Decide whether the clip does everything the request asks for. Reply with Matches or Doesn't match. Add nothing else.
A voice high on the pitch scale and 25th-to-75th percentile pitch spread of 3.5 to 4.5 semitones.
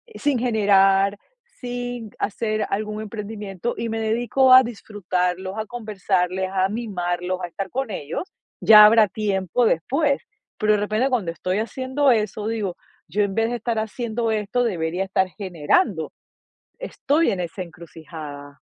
Matches